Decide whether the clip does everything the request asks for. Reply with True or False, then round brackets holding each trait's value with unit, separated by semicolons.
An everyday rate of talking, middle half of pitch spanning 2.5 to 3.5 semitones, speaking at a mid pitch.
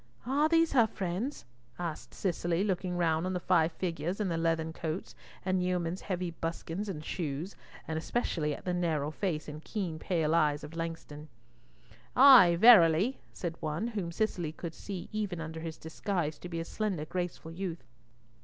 True (170 wpm; 2.9 semitones; 170 Hz)